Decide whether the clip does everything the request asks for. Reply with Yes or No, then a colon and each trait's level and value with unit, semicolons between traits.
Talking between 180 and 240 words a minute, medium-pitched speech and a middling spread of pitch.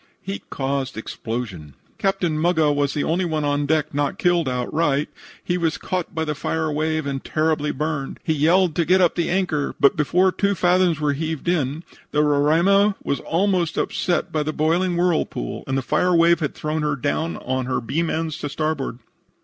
Yes: average, 190 wpm; medium, 155 Hz; average, 3.3 semitones